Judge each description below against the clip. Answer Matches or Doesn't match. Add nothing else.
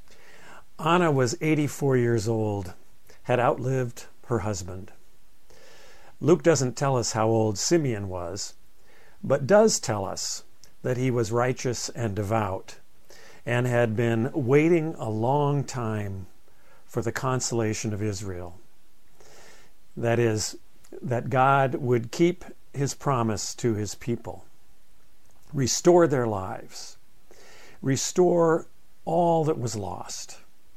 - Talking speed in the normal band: Doesn't match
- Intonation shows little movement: Doesn't match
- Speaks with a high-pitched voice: Doesn't match